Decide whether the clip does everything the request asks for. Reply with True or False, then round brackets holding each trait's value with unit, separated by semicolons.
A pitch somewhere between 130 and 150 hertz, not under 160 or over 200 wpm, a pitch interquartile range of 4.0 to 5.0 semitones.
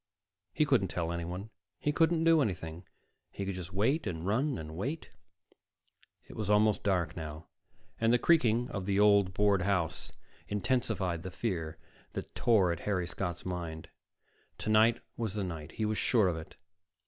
False (100 Hz; 165 wpm; 4.5 semitones)